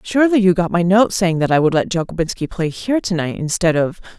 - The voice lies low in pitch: No, medium, 180 Hz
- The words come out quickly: Yes, fast, 245 wpm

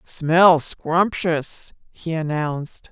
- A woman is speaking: Yes, female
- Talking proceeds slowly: Yes, slow, 80 wpm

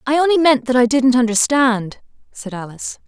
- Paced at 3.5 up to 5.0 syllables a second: No, 5.3 syllables/s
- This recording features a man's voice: No, female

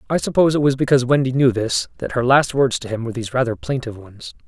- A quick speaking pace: Yes, fast, 255 wpm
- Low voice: Yes, low, 125 Hz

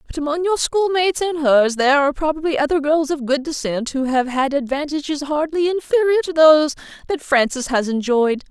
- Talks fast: No, average, 185 wpm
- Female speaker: Yes, female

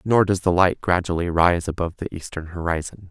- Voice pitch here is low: Yes, very low, 90 Hz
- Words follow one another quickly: No, average, 195 wpm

